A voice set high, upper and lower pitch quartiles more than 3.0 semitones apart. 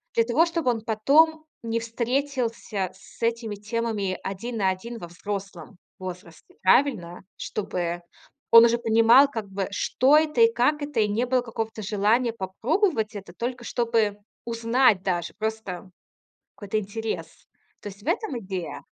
Yes: high, 225 Hz; average, 3.7 semitones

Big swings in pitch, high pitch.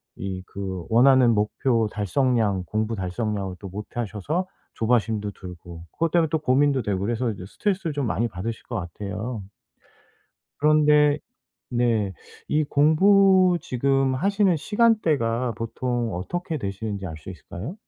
No: wide, 6.7 semitones; low, 120 Hz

